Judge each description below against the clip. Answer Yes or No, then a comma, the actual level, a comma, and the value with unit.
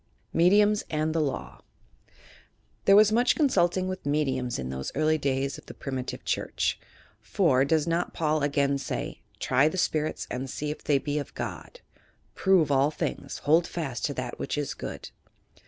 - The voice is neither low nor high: Yes, medium, 150 Hz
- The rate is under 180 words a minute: Yes, average, 170 wpm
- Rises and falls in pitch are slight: No, average, 4.1 semitones